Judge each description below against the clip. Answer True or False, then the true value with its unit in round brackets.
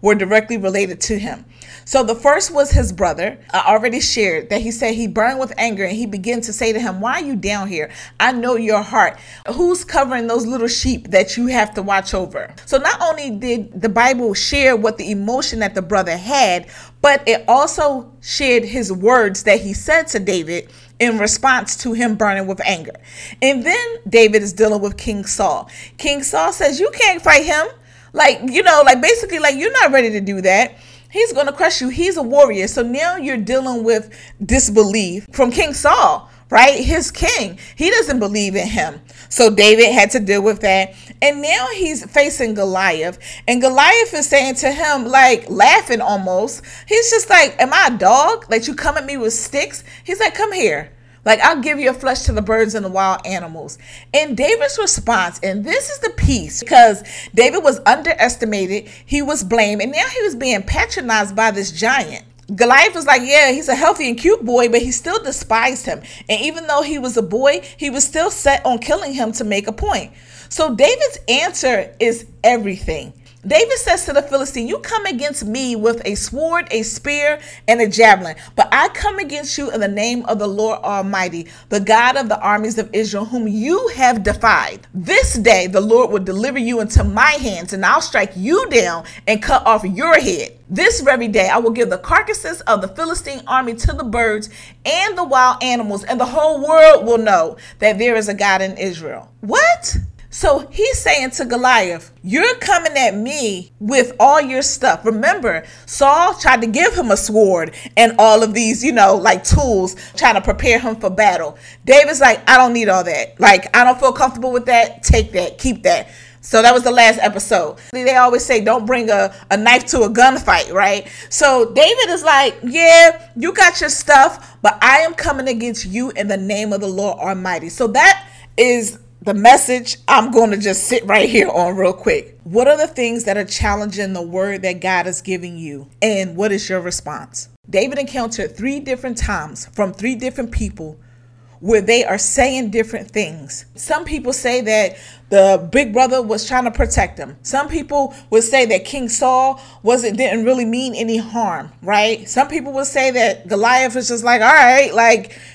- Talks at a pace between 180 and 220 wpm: True (200 wpm)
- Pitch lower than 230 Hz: False (240 Hz)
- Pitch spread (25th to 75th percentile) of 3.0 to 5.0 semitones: False (5.5 semitones)